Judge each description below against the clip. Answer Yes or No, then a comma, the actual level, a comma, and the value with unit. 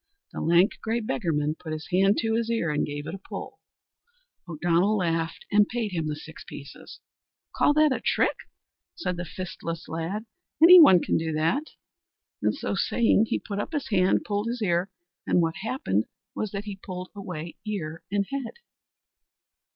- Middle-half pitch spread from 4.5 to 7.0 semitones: Yes, average, 5.0 semitones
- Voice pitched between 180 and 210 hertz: Yes, medium, 185 Hz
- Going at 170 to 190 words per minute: Yes, average, 180 wpm